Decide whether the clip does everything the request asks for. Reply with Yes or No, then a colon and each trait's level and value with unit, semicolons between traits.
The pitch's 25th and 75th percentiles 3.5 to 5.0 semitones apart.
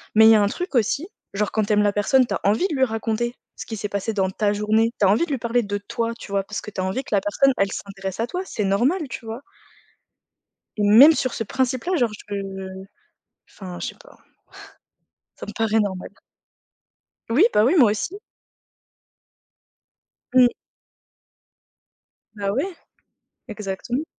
Yes: average, 3.9 semitones